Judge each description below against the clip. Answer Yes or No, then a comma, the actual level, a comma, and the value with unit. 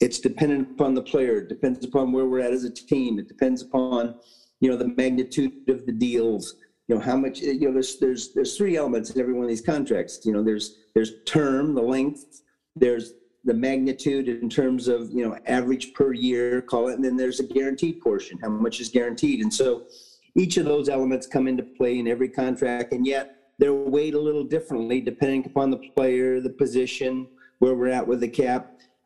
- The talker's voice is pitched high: No, low, 130 Hz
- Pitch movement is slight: Yes, narrow, 1.9 semitones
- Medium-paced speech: No, fast, 210 wpm